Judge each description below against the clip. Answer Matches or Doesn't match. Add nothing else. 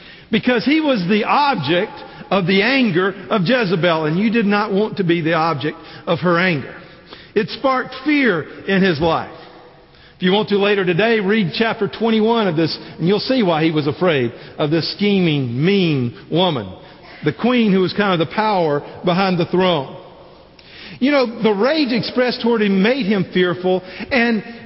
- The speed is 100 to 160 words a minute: Doesn't match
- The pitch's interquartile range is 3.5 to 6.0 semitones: Matches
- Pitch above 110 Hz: Matches